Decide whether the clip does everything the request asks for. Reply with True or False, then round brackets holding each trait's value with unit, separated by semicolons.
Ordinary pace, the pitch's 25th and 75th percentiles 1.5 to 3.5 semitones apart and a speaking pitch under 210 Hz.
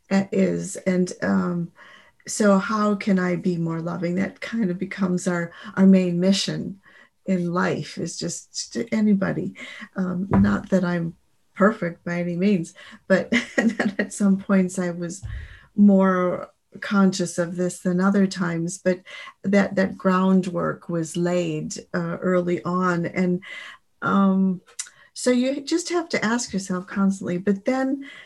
True (140 wpm; 2.5 semitones; 190 Hz)